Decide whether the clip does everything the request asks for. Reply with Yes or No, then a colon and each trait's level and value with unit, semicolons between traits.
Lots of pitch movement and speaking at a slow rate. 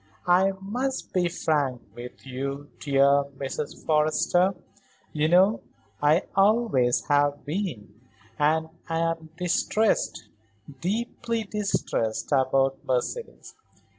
Yes: wide, 5.9 semitones; slow, 95 wpm